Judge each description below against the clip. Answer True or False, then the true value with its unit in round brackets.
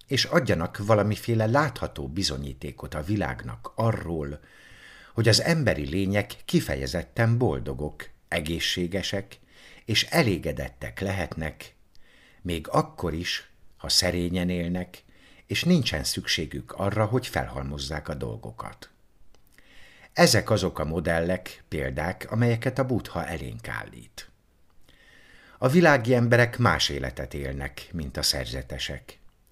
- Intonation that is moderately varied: False (6.9 semitones)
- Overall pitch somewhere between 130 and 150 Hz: False (90 Hz)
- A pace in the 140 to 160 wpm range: False (105 wpm)